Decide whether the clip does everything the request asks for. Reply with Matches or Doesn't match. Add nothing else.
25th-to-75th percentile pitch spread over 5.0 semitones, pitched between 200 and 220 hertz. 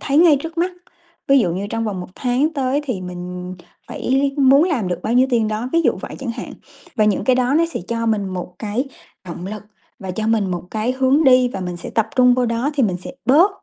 Doesn't match